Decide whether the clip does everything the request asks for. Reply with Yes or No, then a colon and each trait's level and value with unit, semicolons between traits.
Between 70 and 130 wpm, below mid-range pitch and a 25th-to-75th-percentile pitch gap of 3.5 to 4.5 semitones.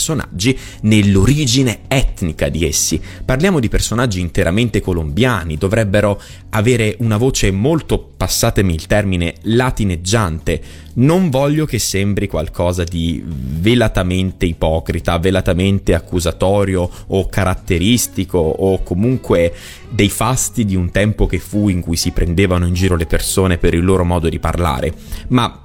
Yes: average, 125 wpm; very low, 95 Hz; average, 3.9 semitones